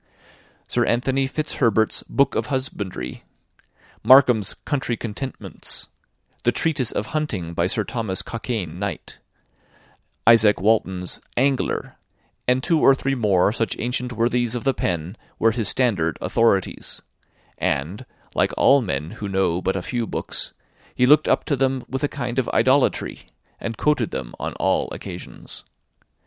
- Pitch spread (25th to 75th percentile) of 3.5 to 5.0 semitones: No, wide, 5.4 semitones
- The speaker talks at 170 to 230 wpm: No, average, 140 wpm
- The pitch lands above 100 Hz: Yes, low, 115 Hz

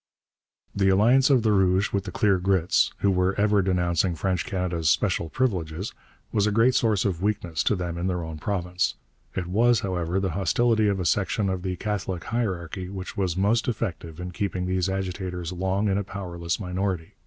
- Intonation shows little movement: Yes, narrow, 2.3 semitones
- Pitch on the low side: Yes, very low, 95 Hz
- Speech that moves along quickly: No, average, 190 wpm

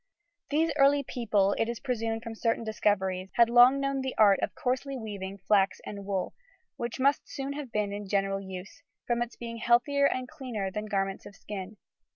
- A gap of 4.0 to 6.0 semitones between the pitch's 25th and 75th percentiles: Yes, average, 4.3 semitones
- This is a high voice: Yes, high, 225 Hz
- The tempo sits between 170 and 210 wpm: Yes, average, 190 wpm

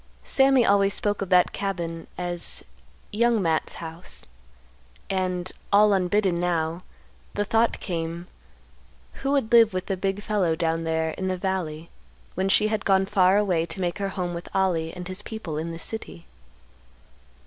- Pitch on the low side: No, medium, 185 Hz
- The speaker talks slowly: No, average, 160 wpm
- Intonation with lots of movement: No, average, 3.2 semitones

